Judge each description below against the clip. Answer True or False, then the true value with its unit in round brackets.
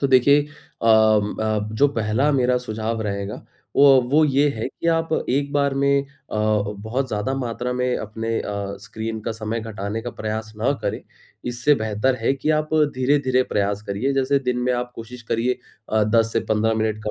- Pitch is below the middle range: True (115 Hz)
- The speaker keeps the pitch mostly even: False (3.8 semitones)